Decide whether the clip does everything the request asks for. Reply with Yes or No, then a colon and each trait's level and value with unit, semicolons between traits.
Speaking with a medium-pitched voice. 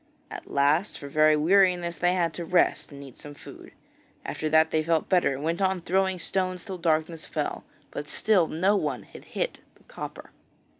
Yes: medium, 170 Hz